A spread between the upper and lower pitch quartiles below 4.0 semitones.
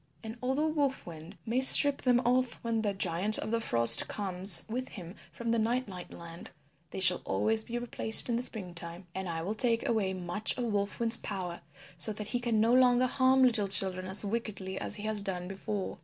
No: average, 4.3 semitones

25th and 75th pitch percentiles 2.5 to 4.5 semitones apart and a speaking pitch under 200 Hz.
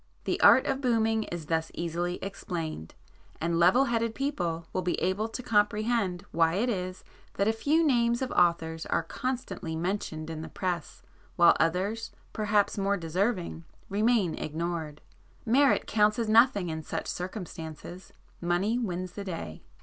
No: average, 4.9 semitones; medium, 185 Hz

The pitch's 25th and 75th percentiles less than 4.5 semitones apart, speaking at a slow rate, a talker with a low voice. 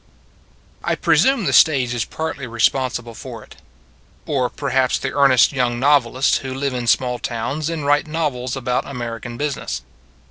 No: average, 2.9 semitones; average, 165 wpm; low, 130 Hz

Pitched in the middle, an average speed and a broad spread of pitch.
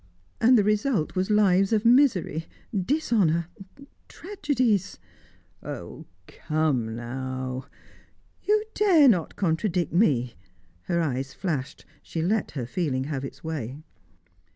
No: medium, 175 Hz; slow, 115 wpm; wide, 8.0 semitones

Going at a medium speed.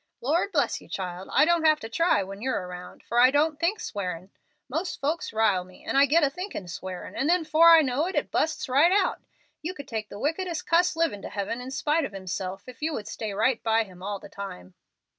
No: fast, 235 wpm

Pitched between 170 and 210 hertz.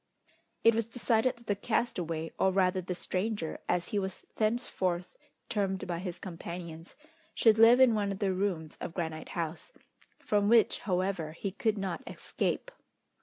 Yes: high, 190 Hz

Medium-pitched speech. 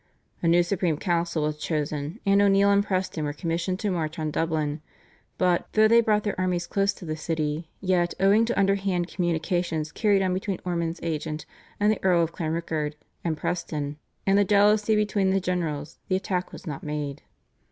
Yes: medium, 175 Hz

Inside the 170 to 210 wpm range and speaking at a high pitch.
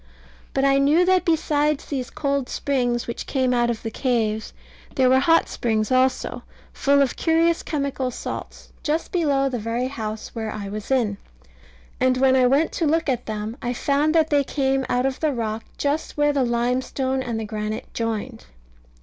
Yes: average, 185 wpm; very high, 260 Hz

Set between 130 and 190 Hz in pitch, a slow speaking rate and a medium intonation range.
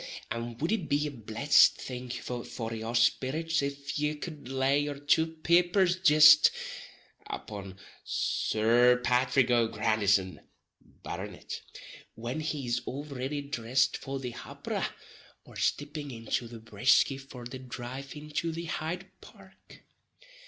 Yes: low, 135 Hz; slow, 130 wpm; average, 4.0 semitones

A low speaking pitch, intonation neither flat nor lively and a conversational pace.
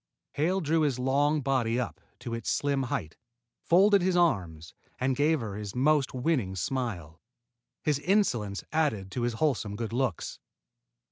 No: low, 130 Hz; wide, 6.0 semitones; average, 150 wpm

